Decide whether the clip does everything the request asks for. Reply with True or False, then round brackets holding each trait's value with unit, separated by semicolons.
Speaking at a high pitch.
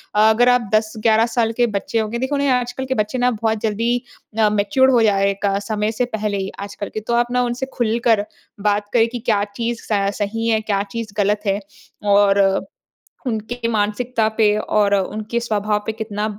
True (220 Hz)